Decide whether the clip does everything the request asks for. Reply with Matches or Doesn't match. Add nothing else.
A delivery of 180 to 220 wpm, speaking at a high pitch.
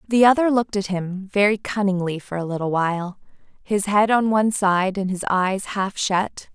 Matches